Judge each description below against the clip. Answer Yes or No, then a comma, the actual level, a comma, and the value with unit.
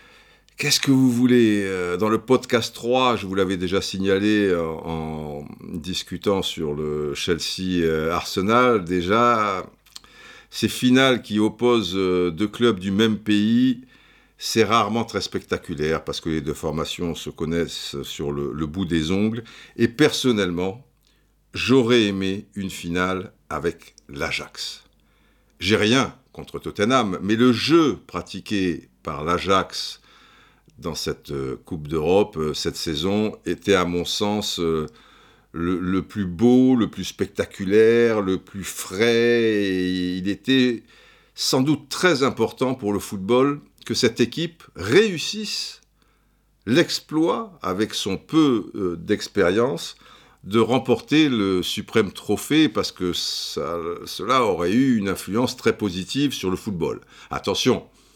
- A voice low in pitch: Yes, low, 105 Hz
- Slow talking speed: Yes, slow, 125 wpm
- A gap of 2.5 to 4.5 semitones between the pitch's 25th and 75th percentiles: No, average, 5.3 semitones